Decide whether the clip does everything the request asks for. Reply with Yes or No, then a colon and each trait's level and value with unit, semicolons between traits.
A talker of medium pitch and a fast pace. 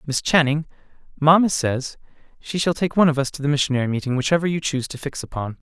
Yes: medium, 145 Hz; fast, 210 wpm